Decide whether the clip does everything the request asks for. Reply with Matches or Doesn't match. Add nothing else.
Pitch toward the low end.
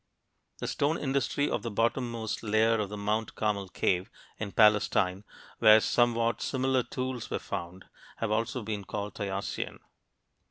Matches